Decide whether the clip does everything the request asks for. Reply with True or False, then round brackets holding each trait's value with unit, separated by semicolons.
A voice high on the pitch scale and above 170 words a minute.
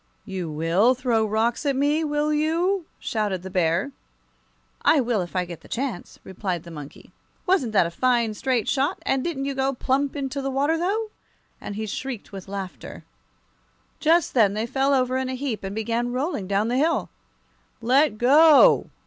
True (250 Hz; 180 wpm)